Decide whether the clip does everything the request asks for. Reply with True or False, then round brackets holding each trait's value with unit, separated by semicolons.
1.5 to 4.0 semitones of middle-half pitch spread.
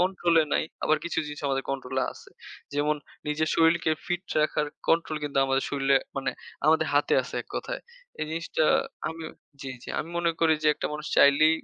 True (2.5 semitones)